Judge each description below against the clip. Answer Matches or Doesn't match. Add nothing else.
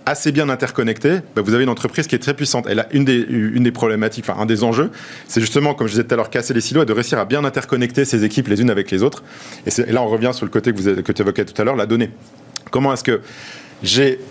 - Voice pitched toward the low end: Matches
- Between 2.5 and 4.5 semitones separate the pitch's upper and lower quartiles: Matches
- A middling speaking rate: Doesn't match